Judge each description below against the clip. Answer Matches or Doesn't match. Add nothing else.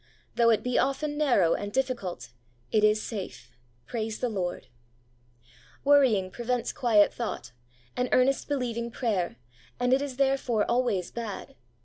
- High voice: Matches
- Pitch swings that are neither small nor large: Matches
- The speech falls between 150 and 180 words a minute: Doesn't match